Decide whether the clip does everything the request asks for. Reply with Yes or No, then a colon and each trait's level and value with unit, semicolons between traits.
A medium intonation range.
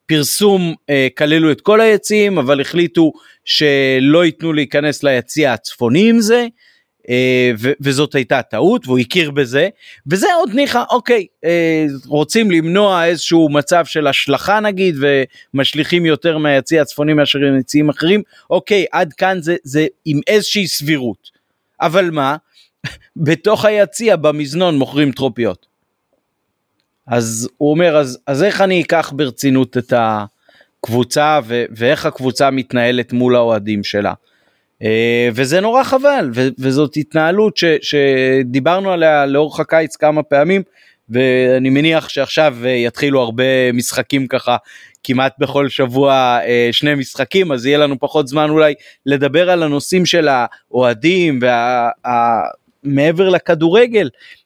Yes: average, 4.6 semitones